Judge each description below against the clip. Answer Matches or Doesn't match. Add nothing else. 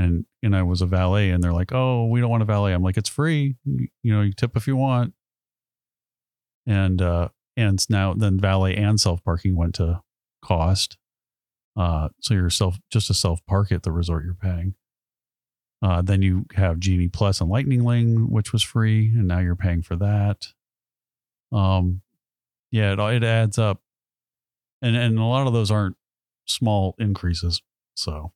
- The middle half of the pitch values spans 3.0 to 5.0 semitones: Matches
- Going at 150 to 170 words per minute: Doesn't match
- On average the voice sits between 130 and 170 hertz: Doesn't match